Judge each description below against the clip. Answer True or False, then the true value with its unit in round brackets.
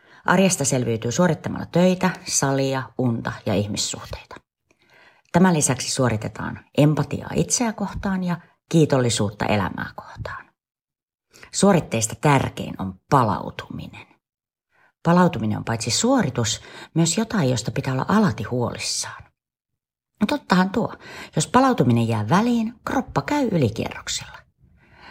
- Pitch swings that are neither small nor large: False (7.9 semitones)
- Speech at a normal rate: True (105 wpm)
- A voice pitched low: False (150 Hz)